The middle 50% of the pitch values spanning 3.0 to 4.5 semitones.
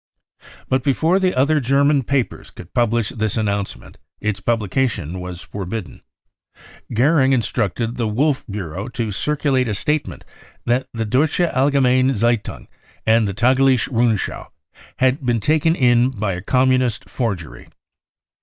Yes: average, 4.0 semitones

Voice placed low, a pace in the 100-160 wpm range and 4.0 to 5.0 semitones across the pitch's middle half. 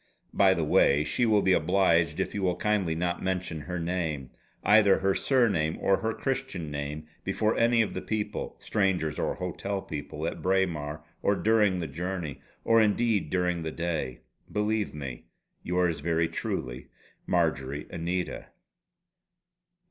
Yes: very low, 90 Hz; average, 150 wpm; average, 4.4 semitones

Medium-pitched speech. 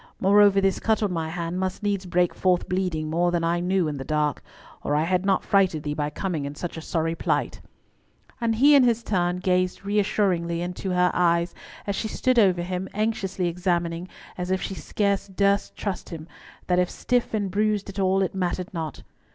Yes: medium, 180 Hz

